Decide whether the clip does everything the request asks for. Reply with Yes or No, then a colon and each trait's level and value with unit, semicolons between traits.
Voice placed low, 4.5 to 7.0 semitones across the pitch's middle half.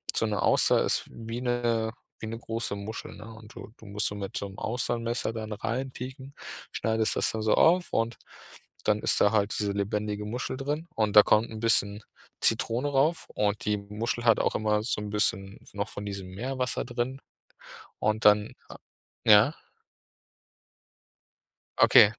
No: low, 110 Hz; narrow, 2.4 semitones